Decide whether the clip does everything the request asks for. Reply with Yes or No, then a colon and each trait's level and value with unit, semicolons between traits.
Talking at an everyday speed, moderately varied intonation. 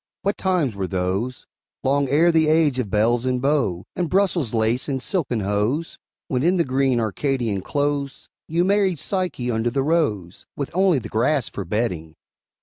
No: average, 170 wpm; wide, 6.3 semitones